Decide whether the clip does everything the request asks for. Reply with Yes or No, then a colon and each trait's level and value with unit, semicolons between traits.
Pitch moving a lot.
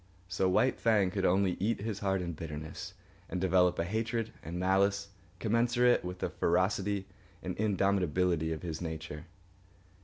No: narrow, 2.6 semitones